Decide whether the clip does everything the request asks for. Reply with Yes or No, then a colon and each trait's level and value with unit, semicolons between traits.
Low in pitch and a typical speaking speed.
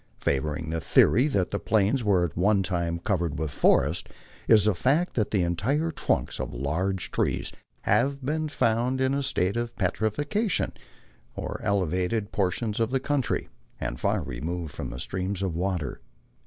Yes: low, 100 Hz; average, 155 wpm